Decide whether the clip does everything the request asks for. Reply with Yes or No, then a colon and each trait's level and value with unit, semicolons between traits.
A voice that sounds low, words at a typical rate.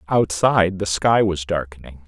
Yes: very low, 90 Hz; average, 145 wpm